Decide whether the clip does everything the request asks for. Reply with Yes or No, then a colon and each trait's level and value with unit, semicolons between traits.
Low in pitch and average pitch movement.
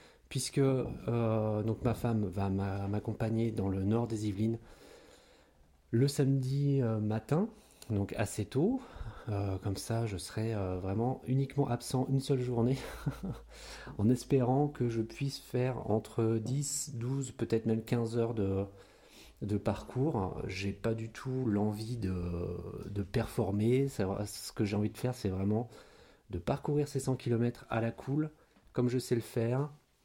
Yes: low, 115 Hz; average, 3.9 semitones